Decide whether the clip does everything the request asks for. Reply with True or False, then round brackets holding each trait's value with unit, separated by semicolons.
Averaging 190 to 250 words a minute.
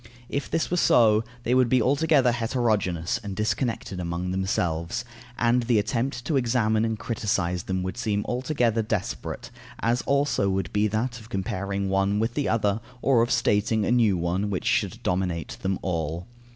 False (170 wpm)